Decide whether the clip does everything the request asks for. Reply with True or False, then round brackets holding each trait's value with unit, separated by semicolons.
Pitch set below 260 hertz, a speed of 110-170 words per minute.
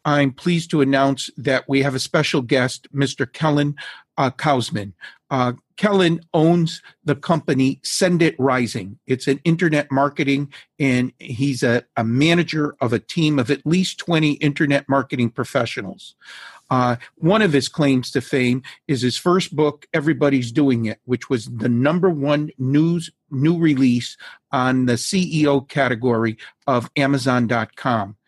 True (140 Hz; 145 wpm)